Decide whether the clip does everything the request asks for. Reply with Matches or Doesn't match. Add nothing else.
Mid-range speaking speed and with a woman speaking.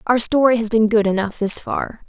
Doesn't match